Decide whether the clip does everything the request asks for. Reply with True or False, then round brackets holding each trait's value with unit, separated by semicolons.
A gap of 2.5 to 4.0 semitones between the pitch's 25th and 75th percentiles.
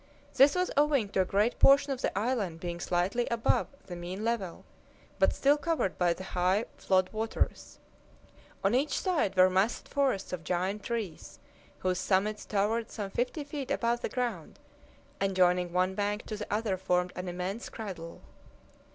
False (4.5 semitones)